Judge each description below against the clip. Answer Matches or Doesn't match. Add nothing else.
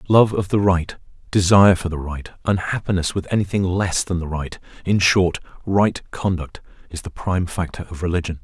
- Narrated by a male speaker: Matches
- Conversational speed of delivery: Matches